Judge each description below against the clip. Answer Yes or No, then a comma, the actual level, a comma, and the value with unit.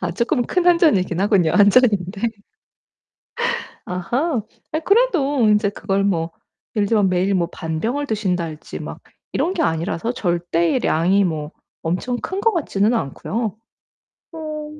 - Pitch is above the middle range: Yes, high, 205 Hz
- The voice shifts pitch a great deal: Yes, wide, 7.3 semitones